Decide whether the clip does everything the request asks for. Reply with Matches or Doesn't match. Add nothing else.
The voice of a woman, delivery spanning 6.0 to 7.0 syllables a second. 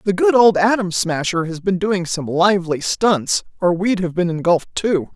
Doesn't match